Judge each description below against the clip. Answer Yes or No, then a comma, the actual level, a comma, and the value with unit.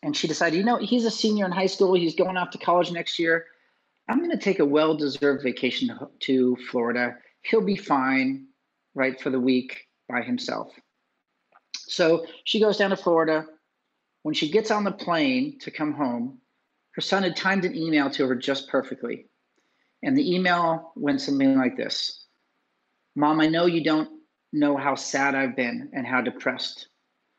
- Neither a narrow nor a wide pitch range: No, wide, 7.0 semitones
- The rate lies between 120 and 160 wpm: No, average, 180 wpm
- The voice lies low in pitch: No, medium, 165 Hz